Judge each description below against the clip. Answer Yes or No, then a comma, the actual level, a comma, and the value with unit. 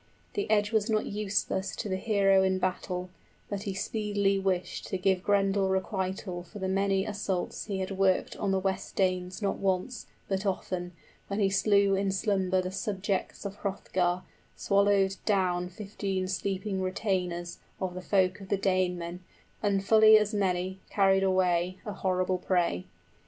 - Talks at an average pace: Yes, average, 165 wpm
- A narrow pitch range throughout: Yes, narrow, 1.4 semitones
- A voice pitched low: No, high, 190 Hz